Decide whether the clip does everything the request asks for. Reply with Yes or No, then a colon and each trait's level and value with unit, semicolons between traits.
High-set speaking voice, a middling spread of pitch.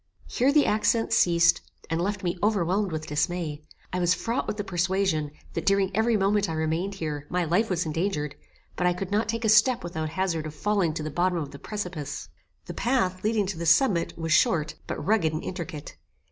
No: medium, 180 Hz; average, 4.2 semitones